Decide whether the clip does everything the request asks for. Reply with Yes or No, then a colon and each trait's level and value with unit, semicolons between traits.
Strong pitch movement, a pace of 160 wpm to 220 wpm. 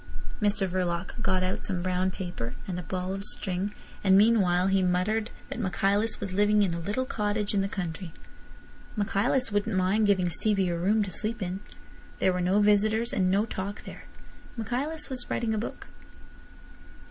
No: narrow, 2.5 semitones; average, 175 wpm